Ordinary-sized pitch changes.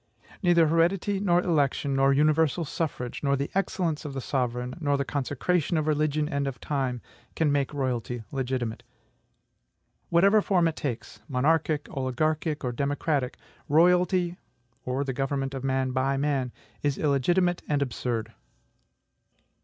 Yes: average, 3.6 semitones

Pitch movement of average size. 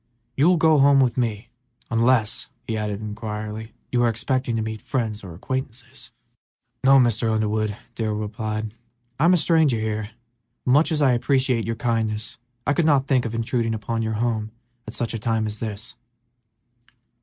Yes: average, 3.2 semitones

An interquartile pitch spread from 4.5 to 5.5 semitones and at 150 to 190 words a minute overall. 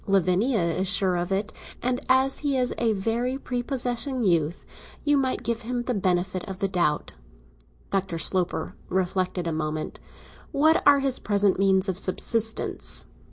Yes: average, 5.2 semitones; average, 155 wpm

